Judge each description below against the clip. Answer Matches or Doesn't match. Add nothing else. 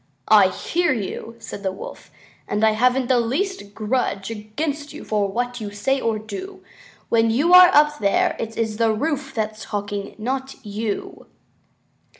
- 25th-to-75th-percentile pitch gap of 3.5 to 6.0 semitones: Matches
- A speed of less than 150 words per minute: Doesn't match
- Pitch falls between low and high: Doesn't match